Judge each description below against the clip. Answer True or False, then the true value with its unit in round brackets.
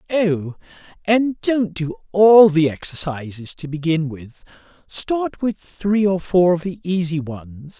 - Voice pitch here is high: False (180 Hz)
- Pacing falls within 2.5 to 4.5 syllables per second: True (3.7 syllables/s)